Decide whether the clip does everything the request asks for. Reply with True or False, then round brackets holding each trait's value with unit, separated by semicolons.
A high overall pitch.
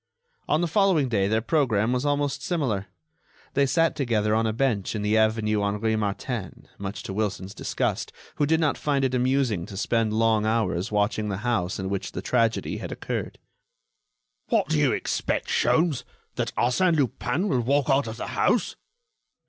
False (115 Hz)